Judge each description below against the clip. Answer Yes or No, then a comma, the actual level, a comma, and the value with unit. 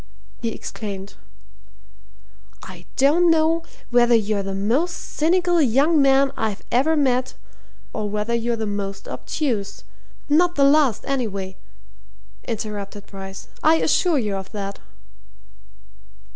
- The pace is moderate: No, slow, 120 wpm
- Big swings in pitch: Yes, wide, 6.7 semitones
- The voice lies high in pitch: Yes, high, 235 Hz